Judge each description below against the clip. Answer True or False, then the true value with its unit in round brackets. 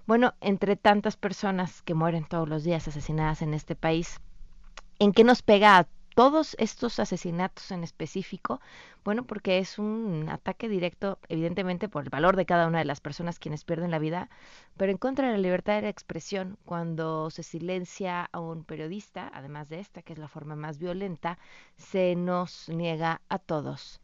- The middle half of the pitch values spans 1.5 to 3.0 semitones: False (3.5 semitones)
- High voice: False (180 Hz)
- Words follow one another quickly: False (180 wpm)